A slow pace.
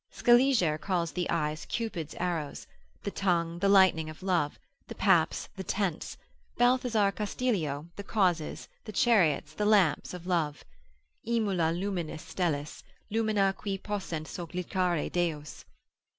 Yes: slow, 125 wpm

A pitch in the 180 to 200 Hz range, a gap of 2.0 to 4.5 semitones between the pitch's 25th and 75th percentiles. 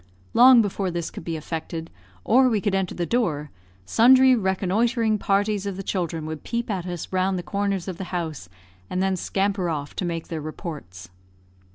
Yes: medium, 185 Hz; average, 3.7 semitones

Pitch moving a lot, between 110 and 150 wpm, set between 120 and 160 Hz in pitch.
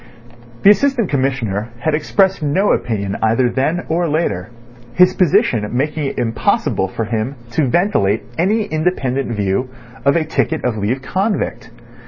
Yes: wide, 7.4 semitones; average, 145 wpm; medium, 140 Hz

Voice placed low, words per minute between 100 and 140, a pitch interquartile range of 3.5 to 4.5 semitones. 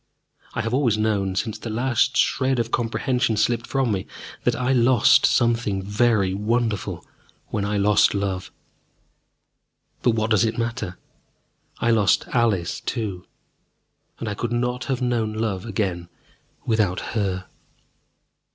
No: low, 110 Hz; slow, 135 wpm; average, 3.0 semitones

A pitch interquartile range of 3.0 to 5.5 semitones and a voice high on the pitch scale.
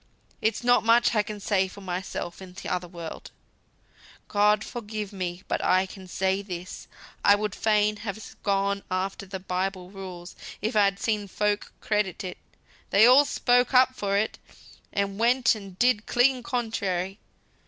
No: narrow, 2.5 semitones; high, 200 Hz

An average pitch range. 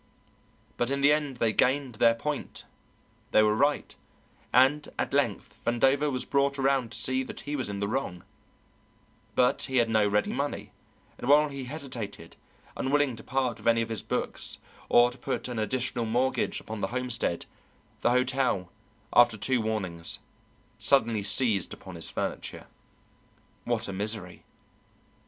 Yes: average, 3.7 semitones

